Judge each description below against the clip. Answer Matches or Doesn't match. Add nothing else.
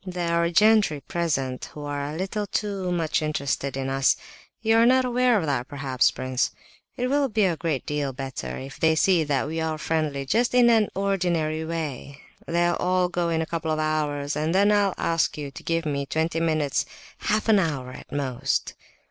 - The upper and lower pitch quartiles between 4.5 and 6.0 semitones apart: Matches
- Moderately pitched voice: Matches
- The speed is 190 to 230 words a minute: Matches